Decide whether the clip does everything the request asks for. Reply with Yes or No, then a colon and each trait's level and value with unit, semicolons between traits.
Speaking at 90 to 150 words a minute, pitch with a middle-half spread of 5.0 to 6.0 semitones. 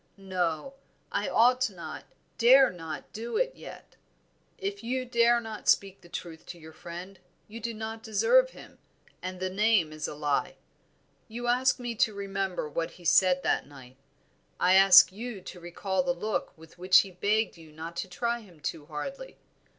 No: average, 175 wpm; average, 5.3 semitones